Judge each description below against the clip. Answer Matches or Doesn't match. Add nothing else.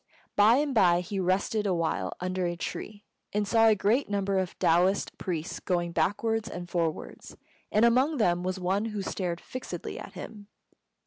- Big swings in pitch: Doesn't match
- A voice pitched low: Doesn't match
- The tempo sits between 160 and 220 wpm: Matches